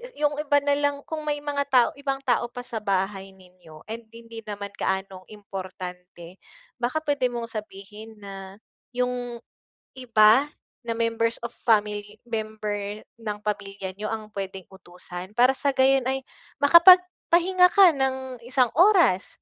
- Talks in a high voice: Yes, high, 230 Hz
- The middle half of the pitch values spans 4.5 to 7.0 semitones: Yes, average, 5.2 semitones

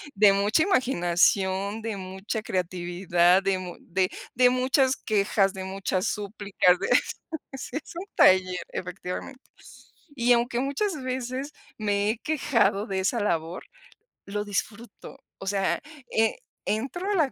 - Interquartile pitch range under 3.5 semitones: No, average, 4.8 semitones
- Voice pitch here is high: Yes, high, 205 Hz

